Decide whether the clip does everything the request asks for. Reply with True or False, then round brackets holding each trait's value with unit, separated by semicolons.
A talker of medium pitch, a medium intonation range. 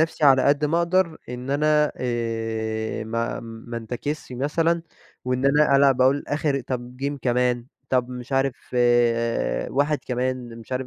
False (130 Hz; 3.1 semitones)